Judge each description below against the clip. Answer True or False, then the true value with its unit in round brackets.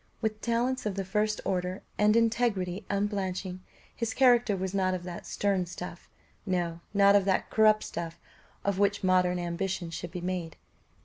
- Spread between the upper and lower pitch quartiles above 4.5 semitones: False (2.8 semitones)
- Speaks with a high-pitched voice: True (195 Hz)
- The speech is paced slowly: False (165 wpm)